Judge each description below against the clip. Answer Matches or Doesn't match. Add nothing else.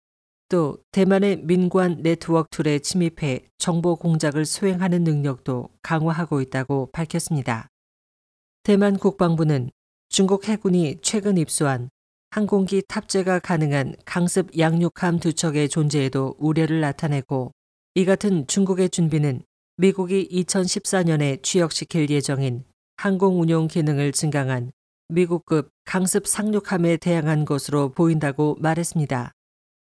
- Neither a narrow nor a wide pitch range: Matches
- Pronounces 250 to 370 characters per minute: Matches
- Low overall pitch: Doesn't match